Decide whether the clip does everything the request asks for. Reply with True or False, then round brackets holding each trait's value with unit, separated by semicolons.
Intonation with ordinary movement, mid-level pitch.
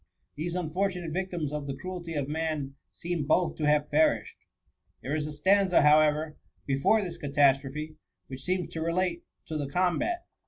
True (3.2 semitones; 155 Hz)